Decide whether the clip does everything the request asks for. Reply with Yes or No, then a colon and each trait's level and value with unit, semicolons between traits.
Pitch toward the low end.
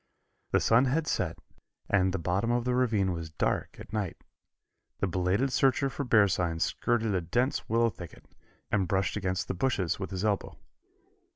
Yes: low, 100 Hz